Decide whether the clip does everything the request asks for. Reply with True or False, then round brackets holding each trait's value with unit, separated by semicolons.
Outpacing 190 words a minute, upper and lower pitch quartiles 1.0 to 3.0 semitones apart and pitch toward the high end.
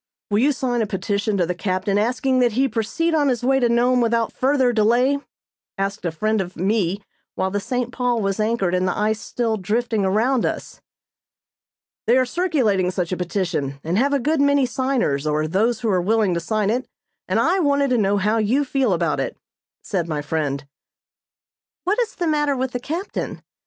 False (200 wpm; 5.3 semitones; 225 Hz)